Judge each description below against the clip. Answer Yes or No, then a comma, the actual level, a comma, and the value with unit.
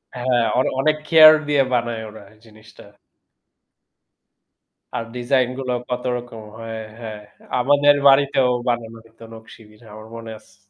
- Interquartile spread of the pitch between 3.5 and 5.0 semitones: No, average, 3.0 semitones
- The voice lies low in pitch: Yes, low, 120 Hz